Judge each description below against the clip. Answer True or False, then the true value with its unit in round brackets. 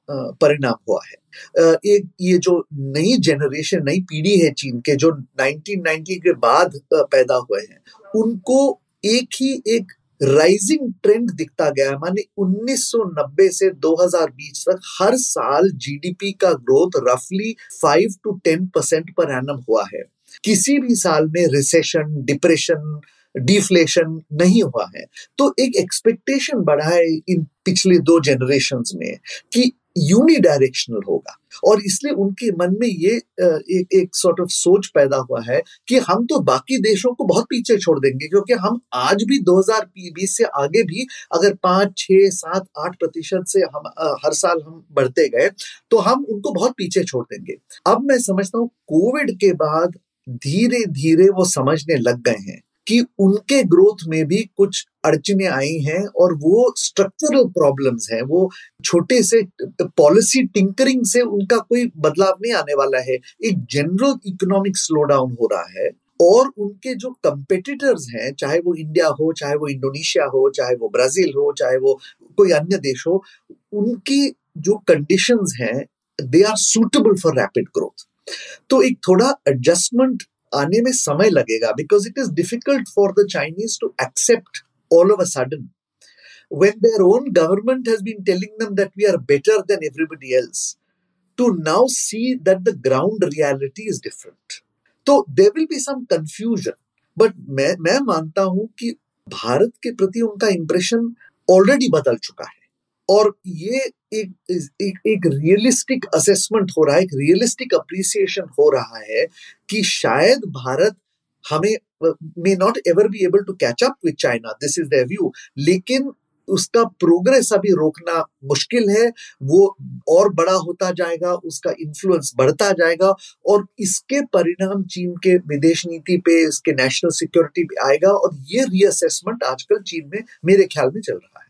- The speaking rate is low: False (135 wpm)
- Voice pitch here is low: False (195 Hz)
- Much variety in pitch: True (6.1 semitones)